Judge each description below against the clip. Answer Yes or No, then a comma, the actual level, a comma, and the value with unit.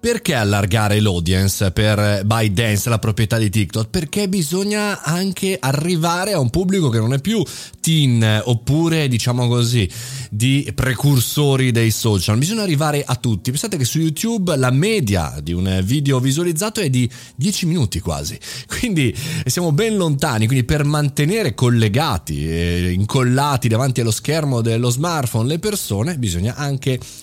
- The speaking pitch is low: Yes, low, 130 Hz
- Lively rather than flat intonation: Yes, wide, 6.2 semitones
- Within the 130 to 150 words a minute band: Yes, average, 145 wpm